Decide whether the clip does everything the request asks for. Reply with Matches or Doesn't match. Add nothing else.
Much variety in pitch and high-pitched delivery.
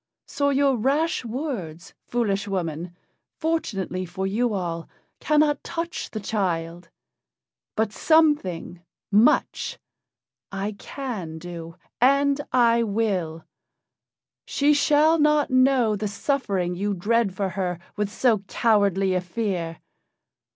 Matches